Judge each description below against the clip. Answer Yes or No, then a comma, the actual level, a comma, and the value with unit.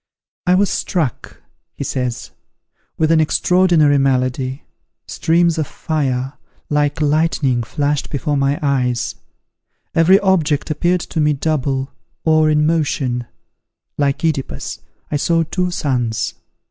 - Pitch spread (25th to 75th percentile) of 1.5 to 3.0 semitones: No, average, 3.4 semitones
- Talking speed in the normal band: No, slow, 120 wpm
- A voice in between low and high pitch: Yes, medium, 150 Hz